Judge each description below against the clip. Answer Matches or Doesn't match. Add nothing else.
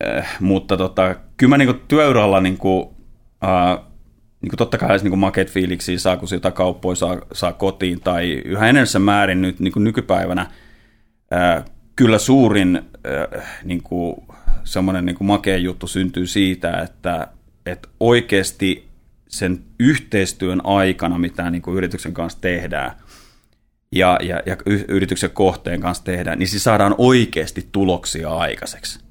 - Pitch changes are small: Matches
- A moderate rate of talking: Matches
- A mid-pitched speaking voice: Doesn't match